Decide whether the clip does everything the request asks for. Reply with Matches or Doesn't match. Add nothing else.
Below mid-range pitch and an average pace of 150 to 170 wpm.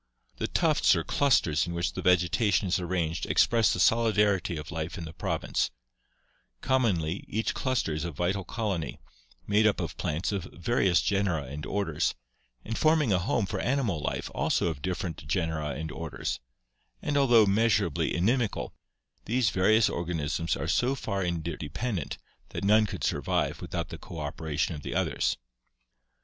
Matches